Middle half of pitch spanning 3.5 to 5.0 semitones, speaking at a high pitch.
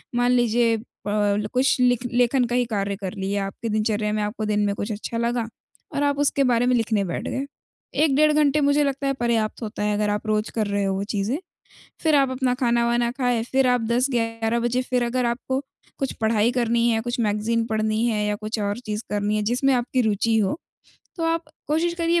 No: average, 3.1 semitones; high, 235 Hz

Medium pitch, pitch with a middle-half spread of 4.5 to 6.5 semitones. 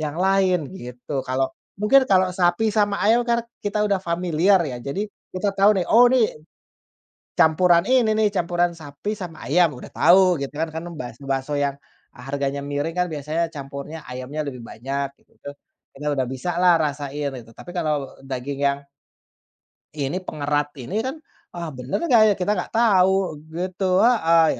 Yes: medium, 165 Hz; average, 5.3 semitones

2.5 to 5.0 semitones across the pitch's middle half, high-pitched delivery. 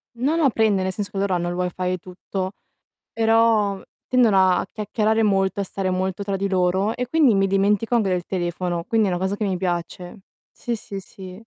Yes: average, 2.9 semitones; high, 195 Hz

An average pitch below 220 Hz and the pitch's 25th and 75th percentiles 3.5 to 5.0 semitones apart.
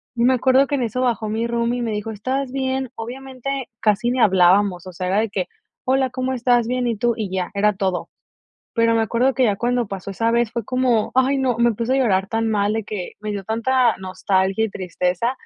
No: high, 230 Hz; average, 3.8 semitones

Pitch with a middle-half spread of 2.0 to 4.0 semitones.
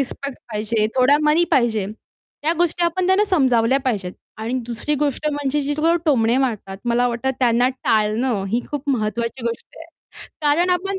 No: average, 4.5 semitones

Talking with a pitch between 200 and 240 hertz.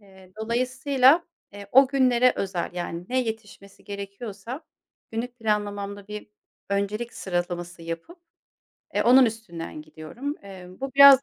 Yes: high, 210 Hz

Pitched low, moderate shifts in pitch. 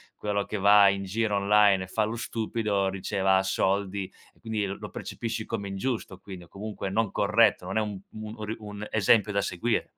No: low, 105 Hz; narrow, 1.9 semitones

